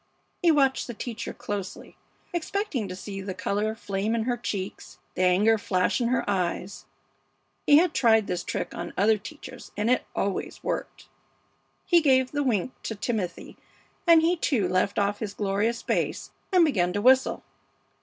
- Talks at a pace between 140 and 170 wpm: Yes, average, 165 wpm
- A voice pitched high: Yes, high, 220 Hz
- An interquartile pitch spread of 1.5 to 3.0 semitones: No, average, 4.9 semitones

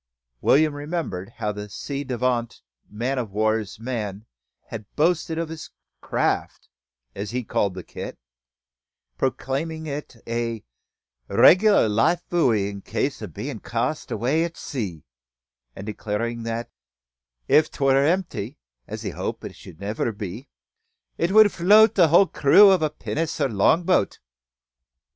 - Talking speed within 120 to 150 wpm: Yes, average, 140 wpm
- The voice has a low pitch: Yes, low, 130 Hz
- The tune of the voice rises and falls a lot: Yes, wide, 7.2 semitones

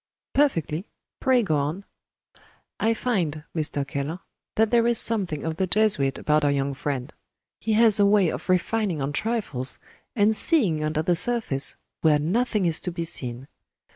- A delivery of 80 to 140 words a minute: No, average, 165 wpm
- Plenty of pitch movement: Yes, wide, 6.8 semitones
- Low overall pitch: No, medium, 170 Hz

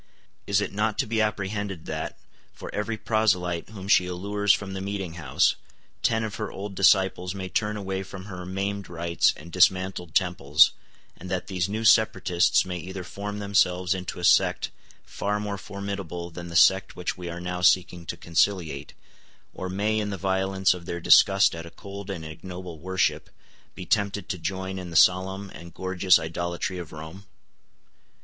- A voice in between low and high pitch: No, very low, 95 Hz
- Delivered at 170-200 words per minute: Yes, average, 175 wpm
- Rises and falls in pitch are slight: Yes, narrow, 2.3 semitones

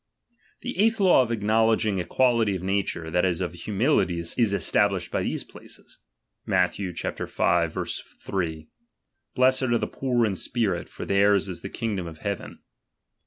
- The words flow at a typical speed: Yes, average, 160 wpm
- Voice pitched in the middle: No, low, 100 Hz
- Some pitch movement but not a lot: Yes, average, 4.7 semitones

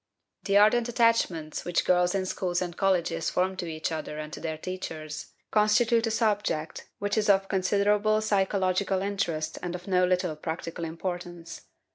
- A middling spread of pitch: Yes, average, 3.4 semitones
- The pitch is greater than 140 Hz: Yes, medium, 185 Hz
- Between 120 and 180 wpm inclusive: Yes, average, 160 wpm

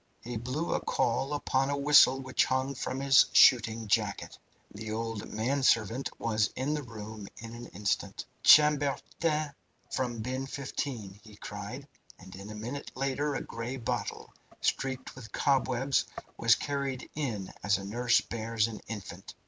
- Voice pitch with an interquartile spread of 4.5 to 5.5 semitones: No, average, 3.9 semitones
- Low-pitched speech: Yes, low, 125 Hz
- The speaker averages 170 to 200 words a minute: No, average, 150 wpm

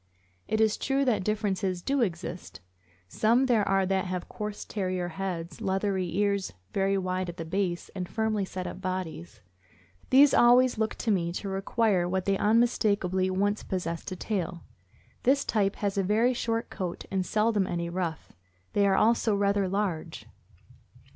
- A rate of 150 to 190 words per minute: Yes, average, 160 wpm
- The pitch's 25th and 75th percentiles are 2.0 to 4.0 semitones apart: Yes, average, 2.8 semitones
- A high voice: Yes, high, 195 Hz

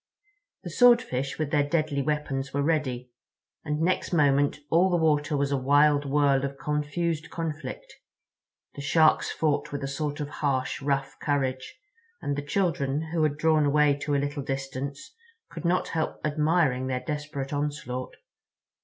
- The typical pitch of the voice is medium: Yes, medium, 145 Hz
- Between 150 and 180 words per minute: Yes, average, 155 wpm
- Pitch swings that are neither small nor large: No, narrow, 2.1 semitones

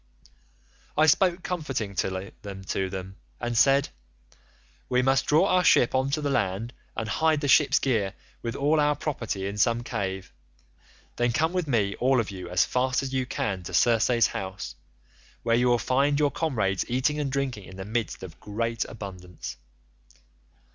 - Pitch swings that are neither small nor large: No, wide, 5.8 semitones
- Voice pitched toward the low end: Yes, low, 120 Hz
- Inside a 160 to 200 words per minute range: Yes, average, 170 wpm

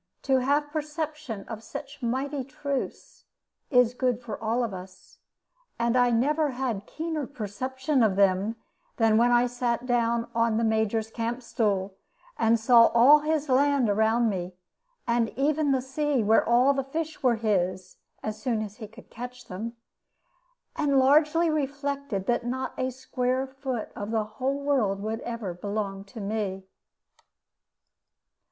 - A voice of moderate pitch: No, high, 240 Hz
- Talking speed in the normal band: Yes, average, 150 wpm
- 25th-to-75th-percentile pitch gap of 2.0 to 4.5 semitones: Yes, average, 3.8 semitones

